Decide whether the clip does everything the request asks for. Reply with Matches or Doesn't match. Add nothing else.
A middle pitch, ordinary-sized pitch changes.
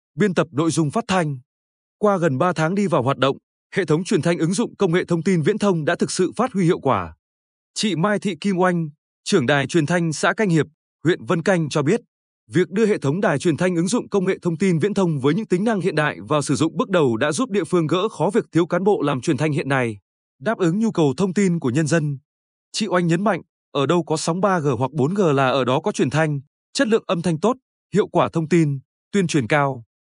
Matches